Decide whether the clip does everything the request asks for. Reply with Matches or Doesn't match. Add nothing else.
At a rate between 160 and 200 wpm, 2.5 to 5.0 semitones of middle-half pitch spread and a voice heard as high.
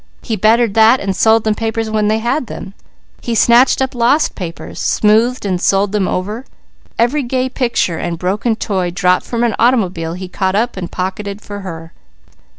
Matches